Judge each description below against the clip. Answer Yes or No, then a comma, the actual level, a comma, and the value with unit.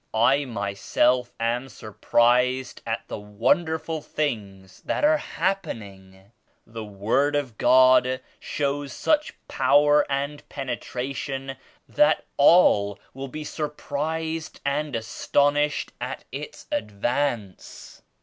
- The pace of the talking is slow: Yes, slow, 110 wpm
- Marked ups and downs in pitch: No, average, 4.6 semitones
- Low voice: Yes, low, 130 Hz